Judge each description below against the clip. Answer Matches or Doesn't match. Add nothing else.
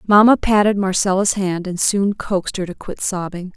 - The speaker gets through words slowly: Doesn't match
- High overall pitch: Matches